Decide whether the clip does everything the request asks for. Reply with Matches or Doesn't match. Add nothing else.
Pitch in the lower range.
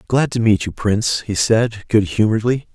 Matches